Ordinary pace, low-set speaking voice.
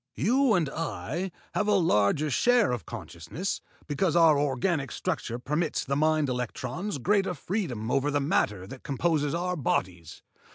No: average, 150 wpm; medium, 150 Hz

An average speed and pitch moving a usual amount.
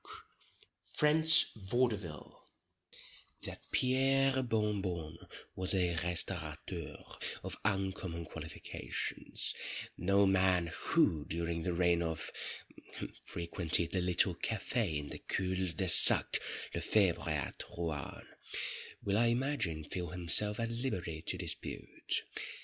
No: slow, 110 wpm; average, 4.0 semitones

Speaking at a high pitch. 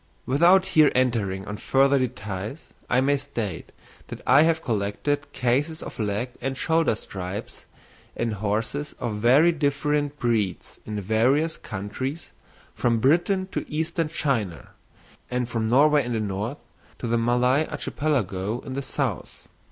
No: low, 125 Hz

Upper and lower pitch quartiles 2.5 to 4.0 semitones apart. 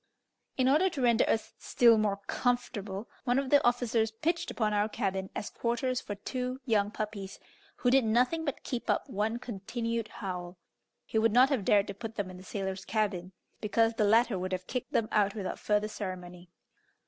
Yes: average, 3.6 semitones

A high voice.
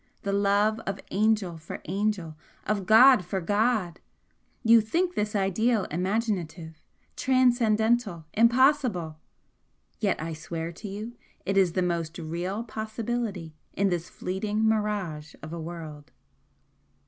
Yes: high, 200 Hz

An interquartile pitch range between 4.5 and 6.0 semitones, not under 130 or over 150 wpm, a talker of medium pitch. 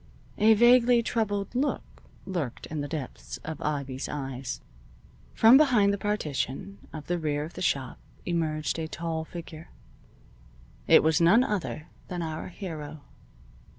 Yes: average, 5.3 semitones; average, 140 wpm; medium, 165 Hz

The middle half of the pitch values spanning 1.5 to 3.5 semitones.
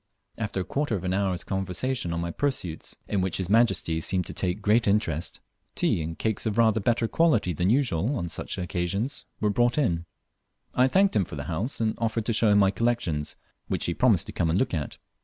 No: average, 5.0 semitones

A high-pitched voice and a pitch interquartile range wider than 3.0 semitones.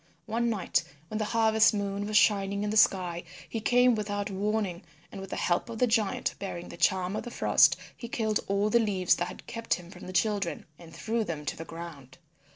Yes: high, 205 Hz; average, 3.4 semitones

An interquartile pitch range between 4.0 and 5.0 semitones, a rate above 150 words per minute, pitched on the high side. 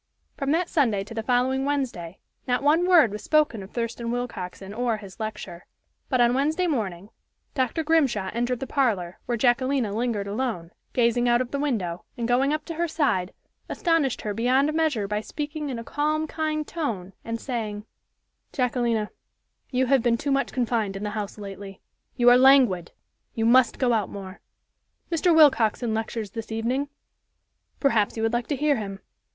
Yes: average, 4.7 semitones; average, 175 wpm; high, 240 Hz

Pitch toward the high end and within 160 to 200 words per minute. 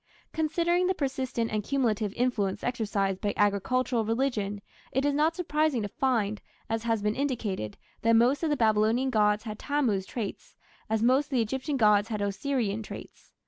Yes: high, 230 Hz; average, 170 wpm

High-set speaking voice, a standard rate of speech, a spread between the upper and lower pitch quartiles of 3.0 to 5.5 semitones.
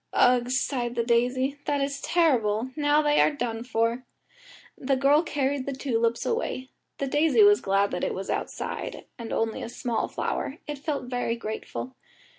Yes: very high, 255 Hz; average, 170 wpm; average, 3.6 semitones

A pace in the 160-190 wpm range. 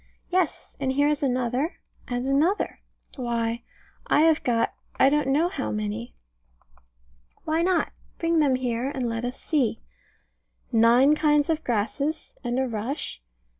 No: average, 140 wpm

